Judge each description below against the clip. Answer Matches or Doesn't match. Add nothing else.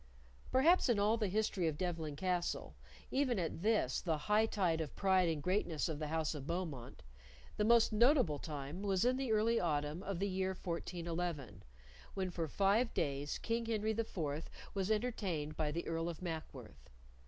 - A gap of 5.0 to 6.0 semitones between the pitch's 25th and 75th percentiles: Matches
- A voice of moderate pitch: Matches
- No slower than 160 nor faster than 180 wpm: Matches